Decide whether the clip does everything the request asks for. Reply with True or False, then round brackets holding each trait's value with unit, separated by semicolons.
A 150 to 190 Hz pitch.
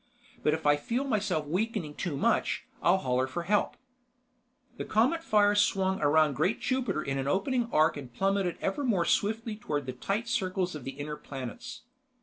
True (185 Hz)